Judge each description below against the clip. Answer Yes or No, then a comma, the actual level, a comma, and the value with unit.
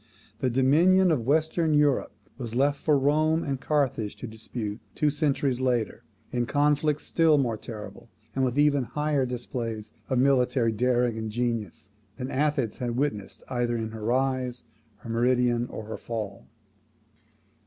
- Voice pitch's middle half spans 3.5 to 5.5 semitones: Yes, average, 3.8 semitones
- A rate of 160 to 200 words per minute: No, average, 150 wpm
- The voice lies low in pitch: Yes, low, 125 Hz